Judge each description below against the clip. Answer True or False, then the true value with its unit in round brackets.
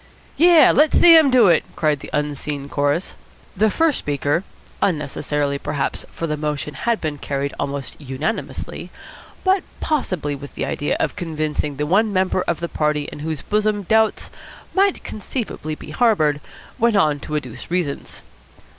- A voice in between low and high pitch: True (155 Hz)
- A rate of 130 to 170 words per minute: True (155 wpm)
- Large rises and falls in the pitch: True (6.6 semitones)